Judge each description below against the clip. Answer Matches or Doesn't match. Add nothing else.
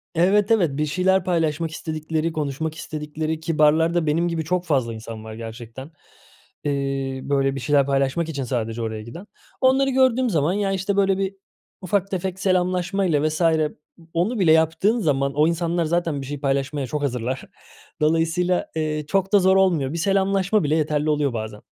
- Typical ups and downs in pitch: Matches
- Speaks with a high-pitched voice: Doesn't match